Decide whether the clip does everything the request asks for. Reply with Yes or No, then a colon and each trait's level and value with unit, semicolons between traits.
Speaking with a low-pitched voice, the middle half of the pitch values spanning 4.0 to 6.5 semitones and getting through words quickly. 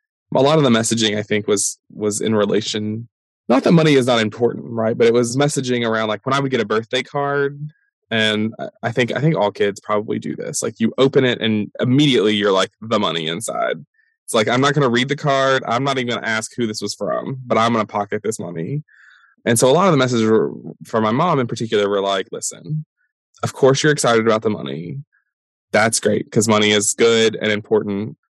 Yes: low, 115 Hz; average, 4.3 semitones; fast, 230 wpm